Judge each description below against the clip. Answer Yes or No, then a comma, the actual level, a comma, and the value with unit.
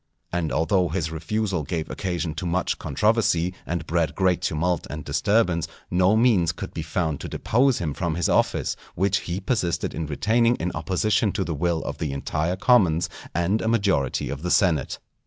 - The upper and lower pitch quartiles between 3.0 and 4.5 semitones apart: Yes, average, 3.6 semitones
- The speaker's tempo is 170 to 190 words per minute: Yes, average, 180 wpm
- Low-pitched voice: Yes, very low, 90 Hz